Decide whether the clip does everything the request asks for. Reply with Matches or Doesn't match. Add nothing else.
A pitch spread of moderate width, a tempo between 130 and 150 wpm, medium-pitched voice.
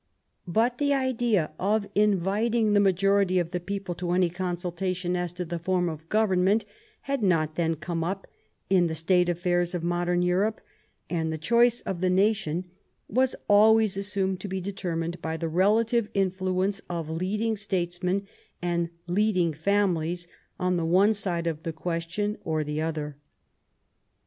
Doesn't match